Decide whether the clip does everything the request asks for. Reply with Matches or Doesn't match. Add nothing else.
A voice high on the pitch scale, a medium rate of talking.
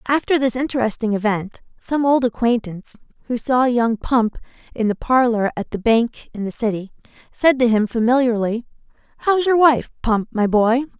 Matches